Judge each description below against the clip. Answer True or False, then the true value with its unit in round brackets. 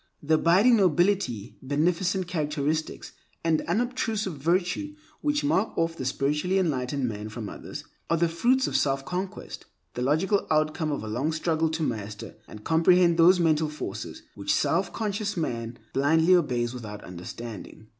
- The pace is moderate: True (155 wpm)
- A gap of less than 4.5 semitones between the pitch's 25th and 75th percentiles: False (5.5 semitones)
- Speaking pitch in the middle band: True (160 Hz)